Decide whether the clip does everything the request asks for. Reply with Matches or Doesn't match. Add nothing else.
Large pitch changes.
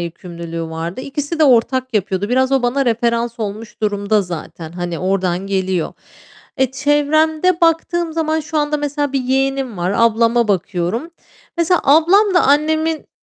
Matches